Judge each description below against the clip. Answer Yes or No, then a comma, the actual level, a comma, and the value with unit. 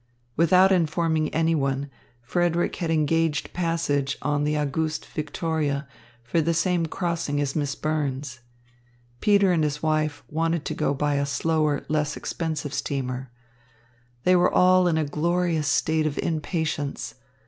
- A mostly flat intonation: Yes, narrow, 2.3 semitones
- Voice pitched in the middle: Yes, medium, 155 Hz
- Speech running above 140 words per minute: No, slow, 135 wpm